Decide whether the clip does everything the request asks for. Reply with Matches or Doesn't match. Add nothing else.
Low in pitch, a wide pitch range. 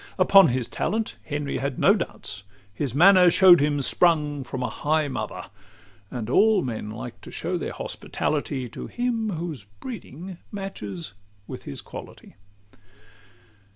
Doesn't match